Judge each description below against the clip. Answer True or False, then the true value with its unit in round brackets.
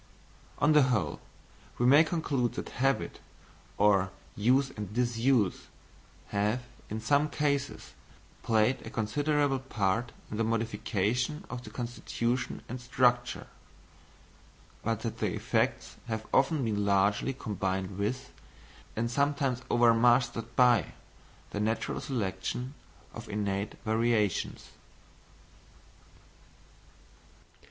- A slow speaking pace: True (105 wpm)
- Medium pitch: False (120 Hz)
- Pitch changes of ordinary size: True (3.7 semitones)